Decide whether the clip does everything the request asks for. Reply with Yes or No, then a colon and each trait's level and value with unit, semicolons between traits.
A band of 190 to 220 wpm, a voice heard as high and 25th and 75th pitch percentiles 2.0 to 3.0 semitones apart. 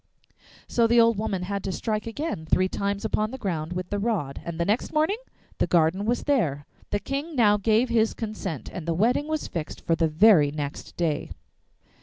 No: average, 200 wpm; high, 205 Hz; wide, 5.4 semitones